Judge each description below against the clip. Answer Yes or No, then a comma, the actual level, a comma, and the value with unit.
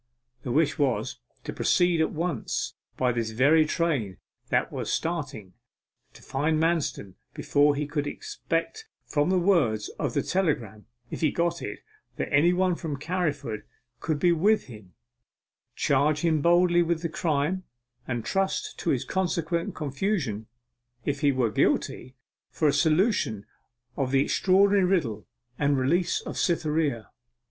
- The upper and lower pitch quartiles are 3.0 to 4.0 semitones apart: No, average, 4.4 semitones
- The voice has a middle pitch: Yes, medium, 155 Hz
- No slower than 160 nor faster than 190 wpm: No, average, 145 wpm